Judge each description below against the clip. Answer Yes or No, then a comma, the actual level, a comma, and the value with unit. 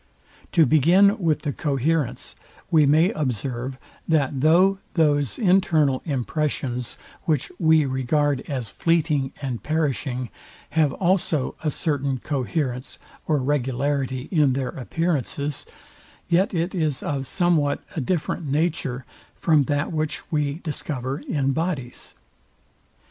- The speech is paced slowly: Yes, slow, 115 wpm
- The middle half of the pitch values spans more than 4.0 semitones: No, average, 3.4 semitones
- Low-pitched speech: No, medium, 145 Hz